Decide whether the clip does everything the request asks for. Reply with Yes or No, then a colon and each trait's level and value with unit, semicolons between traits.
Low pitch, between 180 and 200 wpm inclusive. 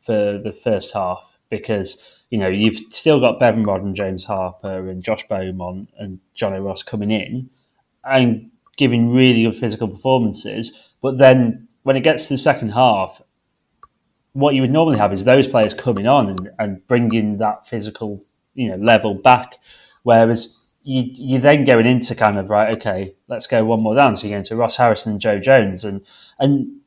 Yes: low, 115 Hz; average, 185 wpm